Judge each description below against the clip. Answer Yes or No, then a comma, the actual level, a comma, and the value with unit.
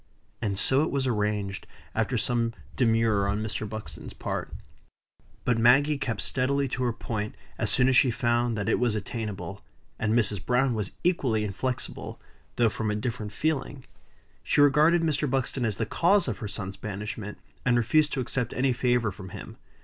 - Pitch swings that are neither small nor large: Yes, average, 3.8 semitones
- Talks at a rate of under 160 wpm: No, average, 180 wpm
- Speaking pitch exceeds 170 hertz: No, low, 120 Hz